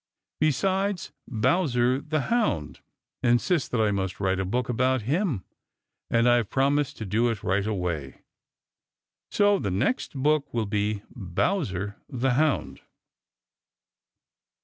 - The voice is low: Yes, low, 120 Hz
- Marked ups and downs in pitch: Yes, wide, 6.4 semitones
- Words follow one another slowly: Yes, slow, 125 wpm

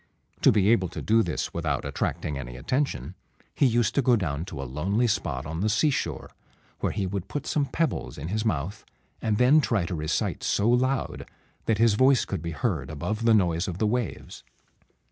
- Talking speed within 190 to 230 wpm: Yes, average, 200 wpm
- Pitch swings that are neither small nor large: No, wide, 6.2 semitones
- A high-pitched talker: No, low, 105 Hz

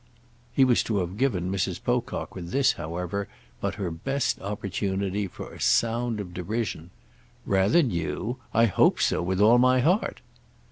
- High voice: No, low, 100 Hz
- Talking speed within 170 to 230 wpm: No, average, 155 wpm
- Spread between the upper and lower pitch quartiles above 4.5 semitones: Yes, average, 5.1 semitones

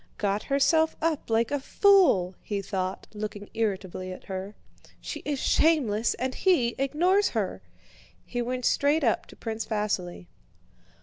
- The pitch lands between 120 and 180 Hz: No, high, 230 Hz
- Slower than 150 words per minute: Yes, average, 140 wpm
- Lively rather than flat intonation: Yes, wide, 6.2 semitones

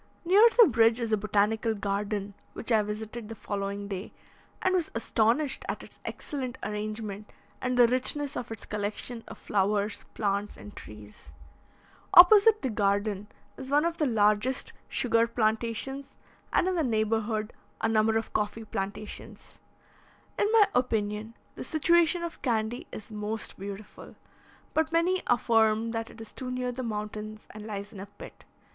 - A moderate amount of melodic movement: Yes, average, 3.3 semitones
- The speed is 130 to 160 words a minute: Yes, average, 155 wpm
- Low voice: No, high, 225 Hz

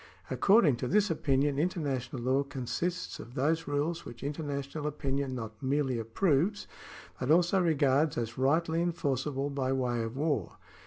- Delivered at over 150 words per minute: No, average, 145 wpm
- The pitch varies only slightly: No, average, 3.7 semitones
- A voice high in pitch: No, medium, 140 Hz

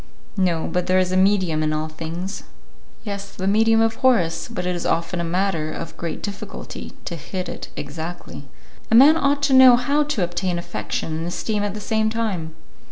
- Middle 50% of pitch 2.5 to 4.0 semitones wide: No, average, 4.7 semitones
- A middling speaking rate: Yes, average, 195 wpm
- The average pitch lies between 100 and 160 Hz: No, medium, 185 Hz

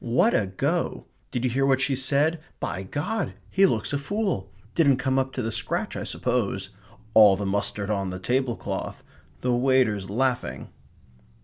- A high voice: No, low, 125 Hz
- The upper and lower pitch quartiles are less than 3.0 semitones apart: No, average, 5.1 semitones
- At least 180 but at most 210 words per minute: No, average, 170 wpm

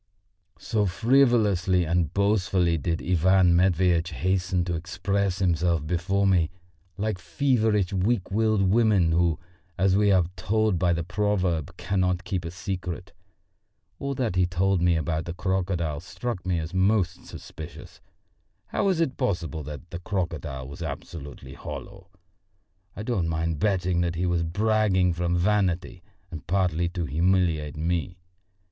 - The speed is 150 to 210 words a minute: No, average, 140 wpm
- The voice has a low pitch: Yes, very low, 90 Hz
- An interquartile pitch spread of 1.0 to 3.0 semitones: Yes, narrow, 2.6 semitones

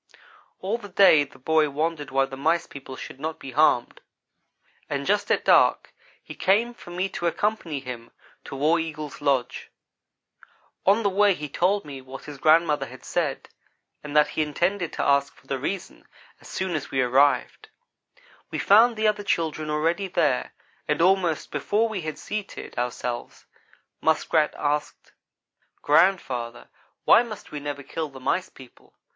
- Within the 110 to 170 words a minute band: Yes, average, 165 wpm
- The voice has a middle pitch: Yes, medium, 155 Hz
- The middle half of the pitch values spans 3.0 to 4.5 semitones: No, average, 5.1 semitones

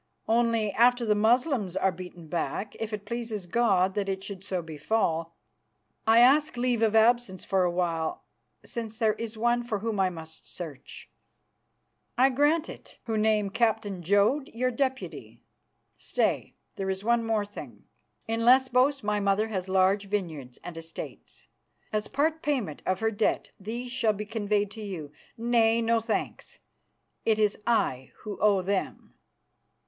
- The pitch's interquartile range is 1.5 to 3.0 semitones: No, average, 3.6 semitones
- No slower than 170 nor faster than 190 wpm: No, average, 155 wpm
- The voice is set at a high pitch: Yes, high, 215 Hz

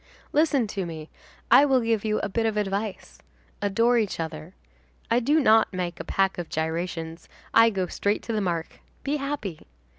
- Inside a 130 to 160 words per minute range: No, average, 180 wpm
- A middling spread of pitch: Yes, average, 4.7 semitones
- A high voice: Yes, high, 205 Hz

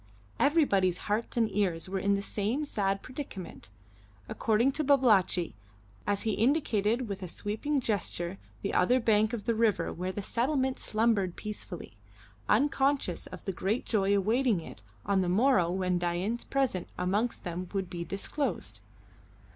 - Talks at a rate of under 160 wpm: Yes, average, 150 wpm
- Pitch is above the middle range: Yes, high, 205 Hz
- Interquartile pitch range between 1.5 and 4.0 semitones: No, average, 4.4 semitones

